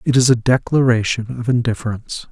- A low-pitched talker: Yes, low, 120 Hz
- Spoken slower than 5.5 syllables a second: No, 6.0 syllables/s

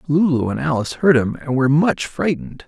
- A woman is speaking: No, male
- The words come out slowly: No, average, 200 wpm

